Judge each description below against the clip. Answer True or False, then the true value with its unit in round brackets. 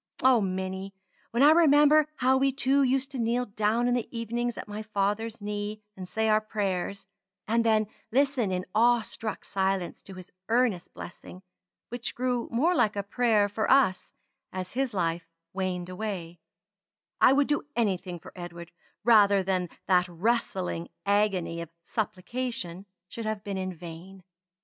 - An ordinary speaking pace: True (160 wpm)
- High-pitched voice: True (210 Hz)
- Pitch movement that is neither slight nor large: True (4.4 semitones)